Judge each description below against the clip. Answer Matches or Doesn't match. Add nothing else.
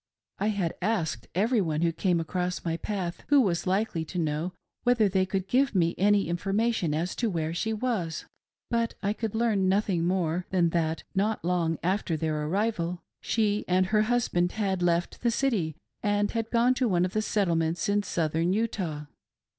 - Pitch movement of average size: Matches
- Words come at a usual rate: Matches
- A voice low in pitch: Doesn't match